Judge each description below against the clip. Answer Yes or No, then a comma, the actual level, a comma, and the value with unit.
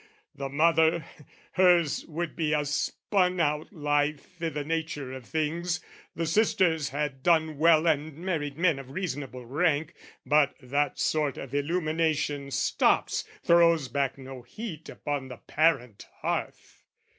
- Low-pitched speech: No, medium, 155 Hz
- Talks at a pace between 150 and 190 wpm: No, slow, 135 wpm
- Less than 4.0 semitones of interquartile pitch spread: Yes, average, 2.9 semitones